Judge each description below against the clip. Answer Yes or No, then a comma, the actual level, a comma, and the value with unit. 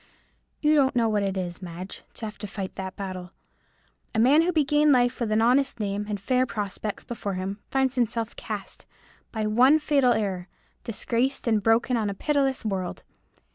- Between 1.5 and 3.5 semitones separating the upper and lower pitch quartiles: No, average, 4.6 semitones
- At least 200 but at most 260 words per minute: No, average, 180 wpm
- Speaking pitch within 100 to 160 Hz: No, high, 225 Hz